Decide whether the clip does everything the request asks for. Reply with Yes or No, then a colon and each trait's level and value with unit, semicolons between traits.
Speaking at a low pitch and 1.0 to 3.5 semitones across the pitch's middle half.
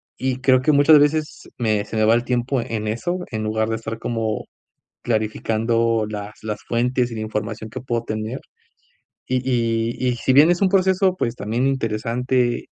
Yes: low, 115 Hz; average, 2.9 semitones